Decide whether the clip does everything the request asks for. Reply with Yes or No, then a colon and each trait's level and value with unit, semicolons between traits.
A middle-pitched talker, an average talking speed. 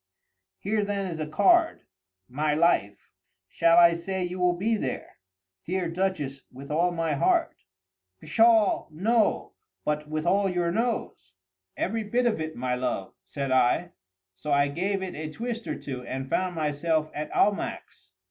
Yes: medium, 170 Hz; average, 150 wpm